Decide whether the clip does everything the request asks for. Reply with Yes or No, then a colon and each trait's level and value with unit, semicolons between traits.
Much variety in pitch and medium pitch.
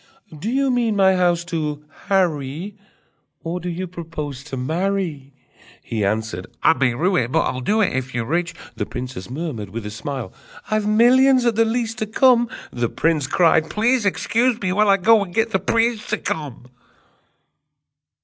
Yes: wide, 7.9 semitones; medium, 175 Hz